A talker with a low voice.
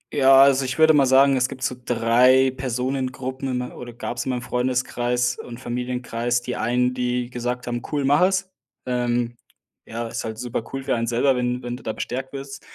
Yes: low, 125 Hz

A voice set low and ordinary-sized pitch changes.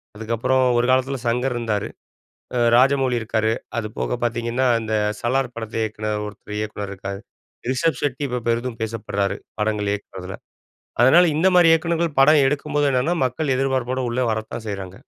Yes: low, 120 Hz; average, 3.7 semitones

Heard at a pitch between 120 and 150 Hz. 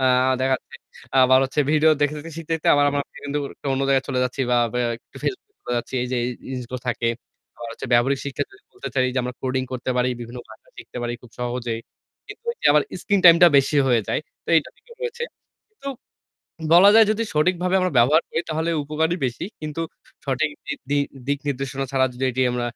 Yes: medium, 140 Hz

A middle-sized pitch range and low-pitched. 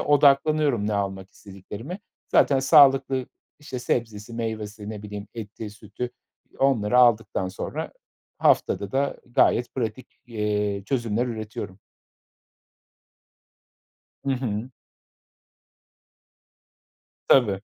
Yes: average, 4.2 semitones; low, 115 Hz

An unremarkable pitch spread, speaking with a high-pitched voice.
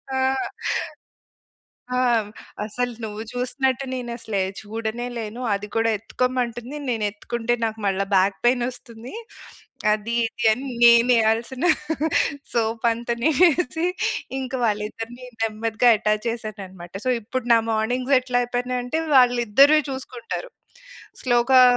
No: narrow, 2.3 semitones; high, 240 Hz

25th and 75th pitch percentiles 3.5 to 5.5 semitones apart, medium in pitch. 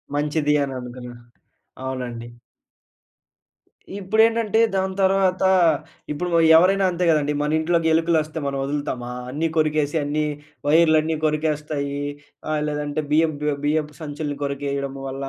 No: narrow, 2.4 semitones; medium, 150 Hz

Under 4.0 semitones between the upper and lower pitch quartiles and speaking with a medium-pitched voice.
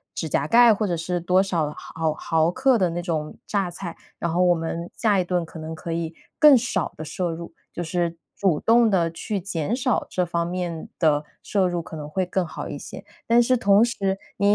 Yes: average, 3.3 semitones; medium, 175 Hz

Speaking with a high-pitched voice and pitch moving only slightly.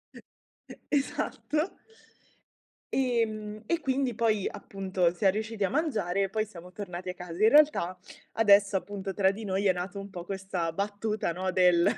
No: high, 200 Hz; average, 3.0 semitones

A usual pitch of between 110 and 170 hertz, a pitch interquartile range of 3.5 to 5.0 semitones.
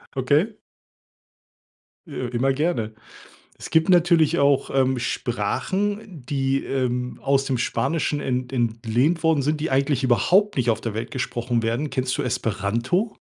Yes: low, 135 Hz; average, 4.5 semitones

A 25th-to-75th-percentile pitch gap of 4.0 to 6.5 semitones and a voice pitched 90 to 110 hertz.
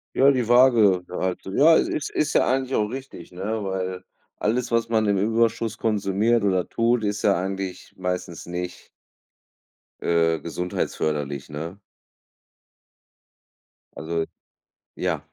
Yes: average, 4.4 semitones; low, 100 Hz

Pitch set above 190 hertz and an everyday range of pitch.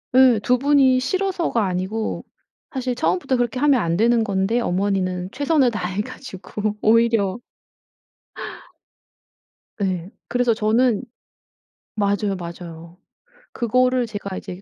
Yes: high, 220 Hz; average, 4.9 semitones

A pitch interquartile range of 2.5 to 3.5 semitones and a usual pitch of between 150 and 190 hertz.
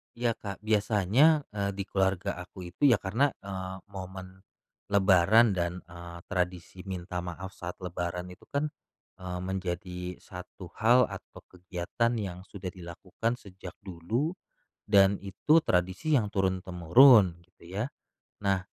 No: average, 2.8 semitones; very low, 95 Hz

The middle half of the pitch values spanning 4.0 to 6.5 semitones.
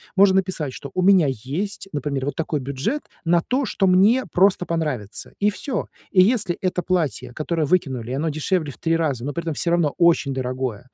Yes: average, 5.1 semitones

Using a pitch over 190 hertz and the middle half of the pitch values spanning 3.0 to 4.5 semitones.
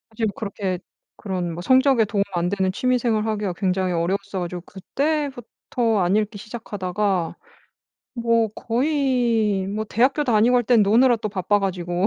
Yes: high, 210 Hz; average, 4.1 semitones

